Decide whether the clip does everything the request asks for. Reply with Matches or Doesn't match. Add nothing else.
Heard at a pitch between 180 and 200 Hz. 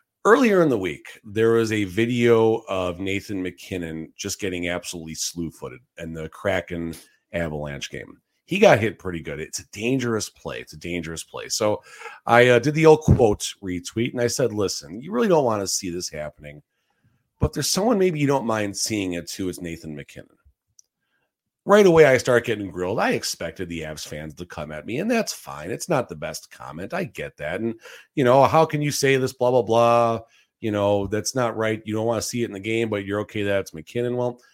Doesn't match